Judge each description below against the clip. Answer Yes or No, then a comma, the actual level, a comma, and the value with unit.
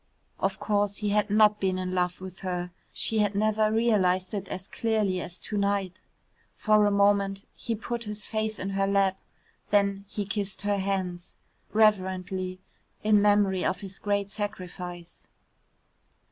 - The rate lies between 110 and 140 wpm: No, average, 155 wpm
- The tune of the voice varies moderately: No, narrow, 1.9 semitones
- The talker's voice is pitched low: No, high, 200 Hz